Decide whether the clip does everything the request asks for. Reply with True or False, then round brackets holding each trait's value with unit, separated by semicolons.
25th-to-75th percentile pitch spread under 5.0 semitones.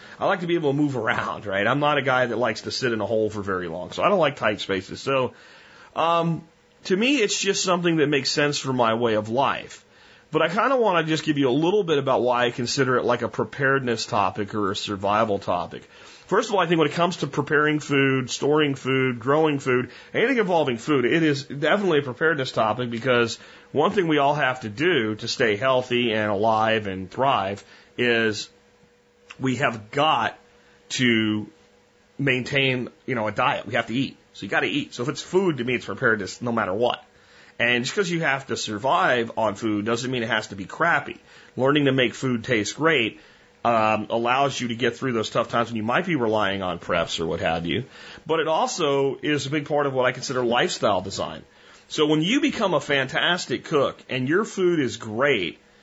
True (4.6 semitones)